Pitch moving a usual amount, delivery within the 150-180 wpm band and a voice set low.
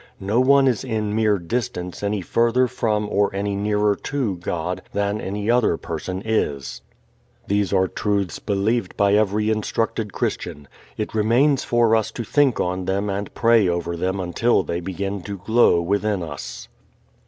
Yes: average, 3.2 semitones; average, 160 wpm; low, 105 Hz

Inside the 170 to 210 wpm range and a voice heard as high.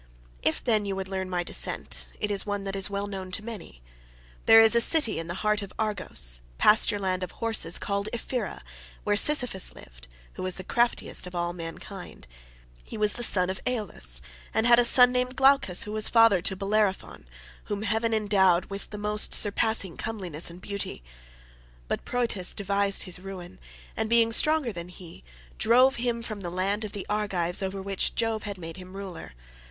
Yes: average, 190 wpm; high, 200 Hz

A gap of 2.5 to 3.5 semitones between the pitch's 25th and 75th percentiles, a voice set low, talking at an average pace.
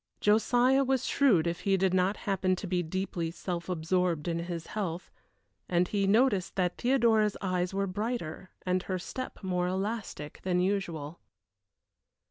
No: average, 2.9 semitones; medium, 185 Hz; average, 145 wpm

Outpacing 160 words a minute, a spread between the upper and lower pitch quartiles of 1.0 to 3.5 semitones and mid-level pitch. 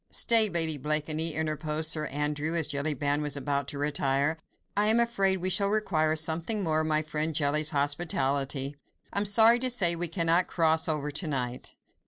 Yes: average, 180 wpm; average, 3.0 semitones; medium, 155 Hz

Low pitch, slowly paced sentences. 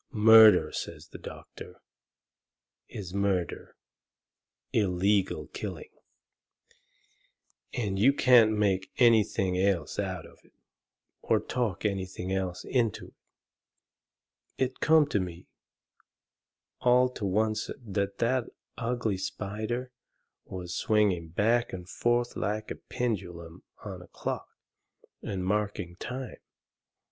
Yes: low, 105 Hz; slow, 105 wpm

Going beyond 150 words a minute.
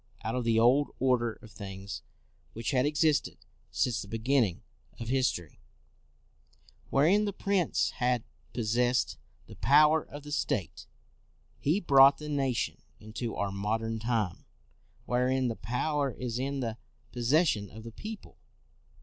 No: average, 140 wpm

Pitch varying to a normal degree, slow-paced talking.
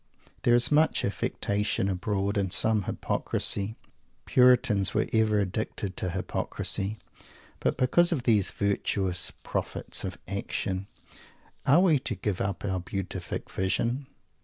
Yes: average, 3.8 semitones; slow, 125 wpm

